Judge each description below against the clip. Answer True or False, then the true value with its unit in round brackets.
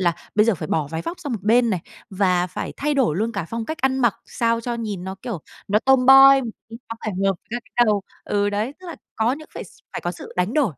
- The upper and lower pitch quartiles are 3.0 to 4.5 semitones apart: False (5.2 semitones)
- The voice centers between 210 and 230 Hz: True (225 Hz)